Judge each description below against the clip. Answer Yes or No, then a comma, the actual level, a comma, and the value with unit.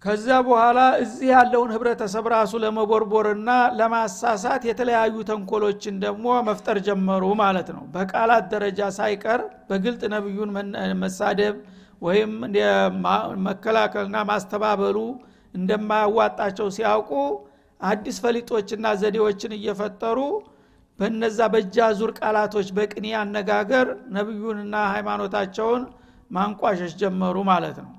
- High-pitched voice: Yes, high, 210 Hz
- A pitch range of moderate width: No, narrow, 1.8 semitones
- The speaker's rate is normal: Yes, average, 90 wpm